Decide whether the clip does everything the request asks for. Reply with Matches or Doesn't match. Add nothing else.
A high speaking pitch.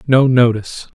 Doesn't match